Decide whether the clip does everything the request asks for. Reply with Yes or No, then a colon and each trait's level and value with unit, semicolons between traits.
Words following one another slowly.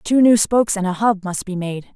No: fast, 275 wpm